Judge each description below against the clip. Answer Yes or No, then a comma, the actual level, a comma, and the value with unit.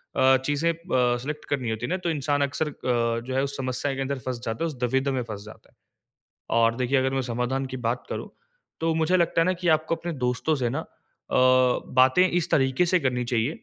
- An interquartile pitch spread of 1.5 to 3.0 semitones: No, average, 4.2 semitones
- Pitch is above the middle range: No, low, 135 Hz